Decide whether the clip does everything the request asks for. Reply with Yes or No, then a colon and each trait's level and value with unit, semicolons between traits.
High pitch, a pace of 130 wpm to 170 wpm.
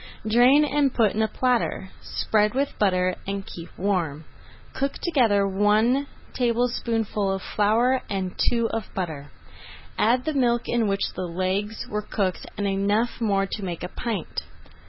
Yes: high, 210 Hz; average, 155 wpm